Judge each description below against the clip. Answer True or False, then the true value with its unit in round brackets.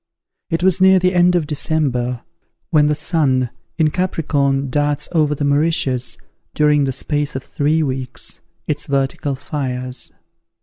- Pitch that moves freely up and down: False (3.0 semitones)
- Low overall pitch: False (145 Hz)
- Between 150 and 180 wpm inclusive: False (140 wpm)